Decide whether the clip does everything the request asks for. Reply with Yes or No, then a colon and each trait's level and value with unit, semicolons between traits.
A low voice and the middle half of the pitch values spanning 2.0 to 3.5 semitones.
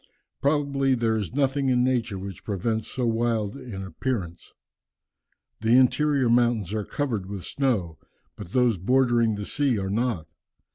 No: low, 115 Hz; average, 4.2 semitones